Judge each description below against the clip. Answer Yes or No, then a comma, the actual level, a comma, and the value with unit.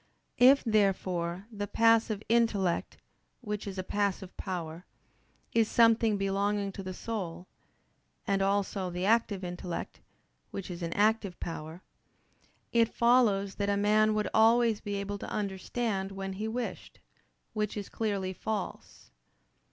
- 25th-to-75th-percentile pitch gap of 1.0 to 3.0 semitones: Yes, narrow, 2.6 semitones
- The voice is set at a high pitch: Yes, high, 200 Hz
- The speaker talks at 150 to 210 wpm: No, slow, 135 wpm